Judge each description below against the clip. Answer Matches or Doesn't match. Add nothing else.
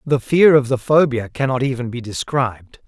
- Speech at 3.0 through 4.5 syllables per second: Doesn't match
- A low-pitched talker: Matches